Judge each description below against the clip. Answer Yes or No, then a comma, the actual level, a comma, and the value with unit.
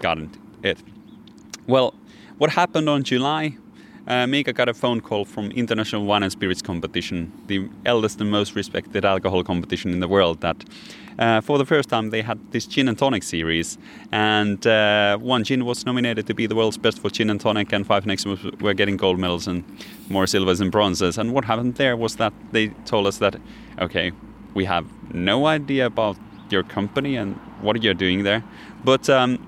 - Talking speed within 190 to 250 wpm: Yes, average, 195 wpm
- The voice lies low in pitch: Yes, low, 105 Hz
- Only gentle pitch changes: No, average, 3.9 semitones